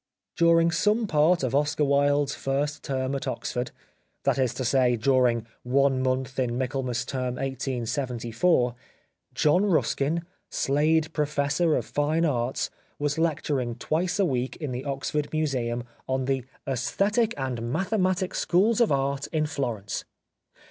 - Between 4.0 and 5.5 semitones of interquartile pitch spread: No, average, 3.6 semitones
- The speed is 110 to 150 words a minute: Yes, average, 145 wpm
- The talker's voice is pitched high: No, medium, 140 Hz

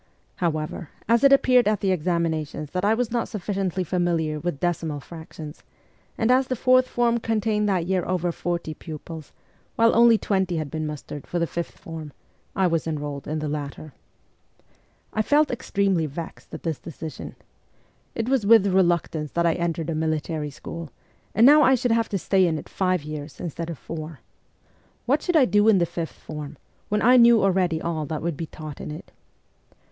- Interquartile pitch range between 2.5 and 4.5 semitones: No, wide, 5.4 semitones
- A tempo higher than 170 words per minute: Yes, average, 185 wpm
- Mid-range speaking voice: Yes, medium, 175 Hz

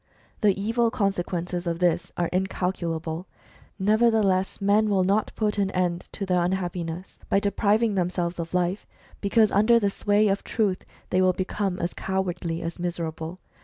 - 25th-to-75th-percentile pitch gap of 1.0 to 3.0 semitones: Yes, average, 2.7 semitones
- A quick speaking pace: No, average, 155 wpm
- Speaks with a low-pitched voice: No, medium, 185 Hz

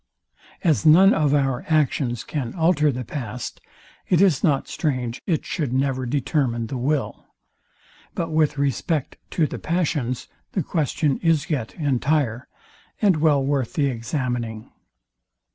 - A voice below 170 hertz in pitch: Yes, medium, 140 Hz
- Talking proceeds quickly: No, slow, 135 wpm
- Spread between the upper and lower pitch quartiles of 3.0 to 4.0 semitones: Yes, average, 3.7 semitones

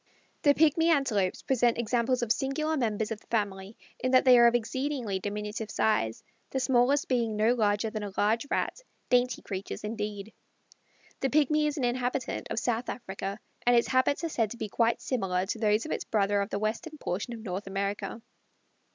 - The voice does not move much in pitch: No, average, 3.6 semitones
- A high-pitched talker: Yes, high, 230 Hz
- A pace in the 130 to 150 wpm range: No, average, 190 wpm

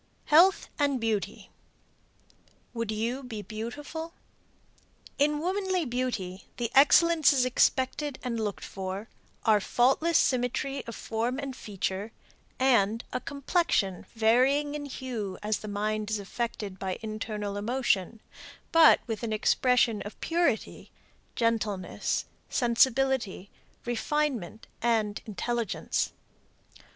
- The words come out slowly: Yes, slow, 105 wpm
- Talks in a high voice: Yes, high, 235 Hz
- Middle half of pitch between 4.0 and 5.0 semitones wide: Yes, average, 4.3 semitones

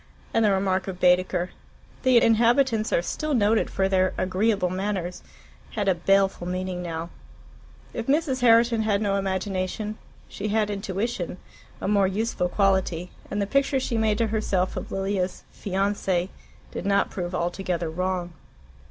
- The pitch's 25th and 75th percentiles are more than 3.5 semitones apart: No, average, 2.9 semitones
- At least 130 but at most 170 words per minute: Yes, average, 150 wpm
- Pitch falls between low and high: No, high, 195 Hz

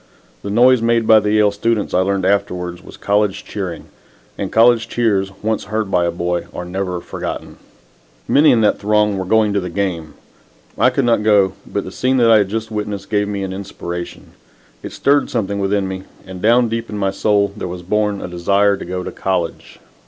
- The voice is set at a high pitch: No, low, 100 Hz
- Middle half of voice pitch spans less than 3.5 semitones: Yes, narrow, 2.6 semitones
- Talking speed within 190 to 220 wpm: Yes, fast, 205 wpm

